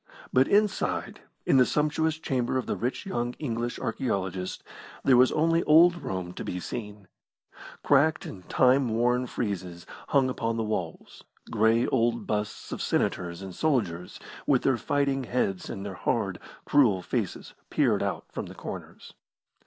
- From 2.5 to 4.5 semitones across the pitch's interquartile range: No, wide, 5.5 semitones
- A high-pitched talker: No, low, 120 Hz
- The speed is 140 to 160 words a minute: Yes, average, 155 wpm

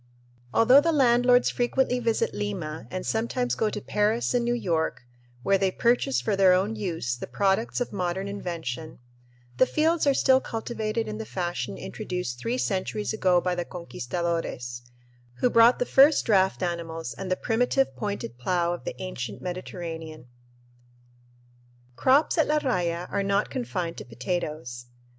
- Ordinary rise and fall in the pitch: No, wide, 5.9 semitones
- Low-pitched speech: No, high, 190 Hz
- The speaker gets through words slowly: No, average, 155 wpm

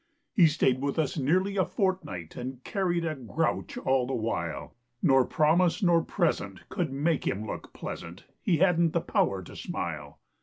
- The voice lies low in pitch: No, medium, 150 Hz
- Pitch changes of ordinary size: No, wide, 7.0 semitones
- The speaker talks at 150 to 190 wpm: Yes, average, 165 wpm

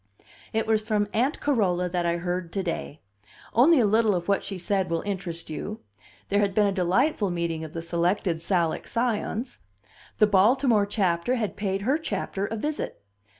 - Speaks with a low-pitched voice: No, high, 200 Hz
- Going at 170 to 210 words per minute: Yes, average, 180 wpm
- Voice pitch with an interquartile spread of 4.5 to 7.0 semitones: No, average, 4.0 semitones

